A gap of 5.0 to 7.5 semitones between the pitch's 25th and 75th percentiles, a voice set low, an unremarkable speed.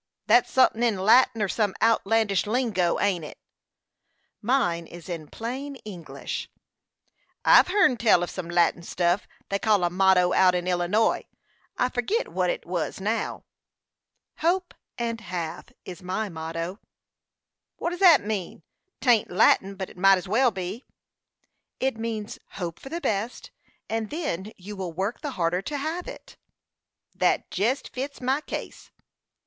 No: wide, 5.5 semitones; high, 210 Hz; average, 150 wpm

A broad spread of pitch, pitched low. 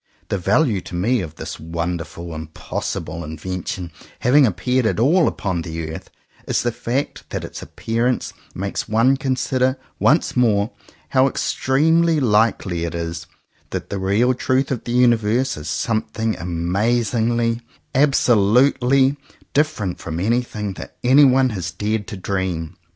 Yes: wide, 6.2 semitones; low, 110 Hz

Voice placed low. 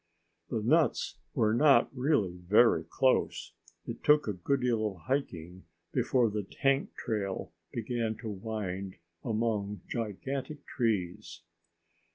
Yes: low, 110 Hz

